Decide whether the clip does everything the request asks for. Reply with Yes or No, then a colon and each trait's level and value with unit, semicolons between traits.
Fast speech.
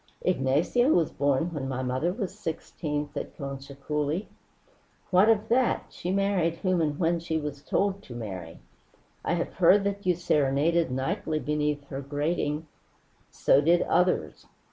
No: average, 155 wpm